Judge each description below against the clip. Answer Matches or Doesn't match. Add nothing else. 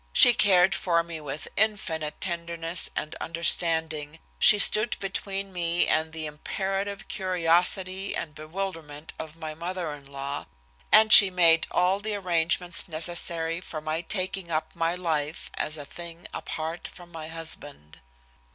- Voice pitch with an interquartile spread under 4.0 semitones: Matches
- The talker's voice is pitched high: Doesn't match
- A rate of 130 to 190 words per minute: Matches